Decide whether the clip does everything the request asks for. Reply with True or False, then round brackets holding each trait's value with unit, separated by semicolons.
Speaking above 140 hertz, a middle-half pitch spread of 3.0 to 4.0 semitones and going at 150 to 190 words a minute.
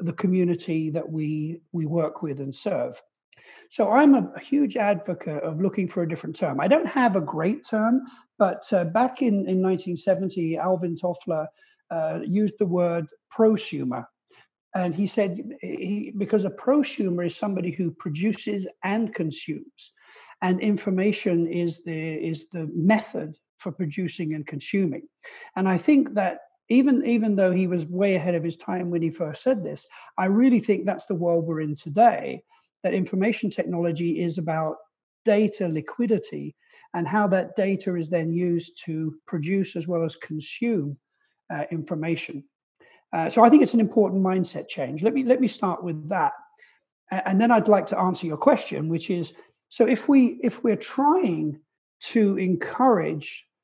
False (185 Hz; 5.0 semitones; 165 wpm)